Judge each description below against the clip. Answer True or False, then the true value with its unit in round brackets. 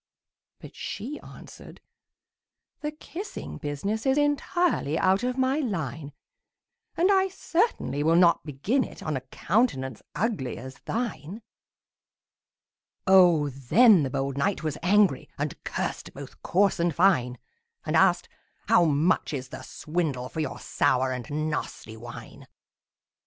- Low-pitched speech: False (170 Hz)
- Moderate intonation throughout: False (8.9 semitones)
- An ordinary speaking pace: False (130 wpm)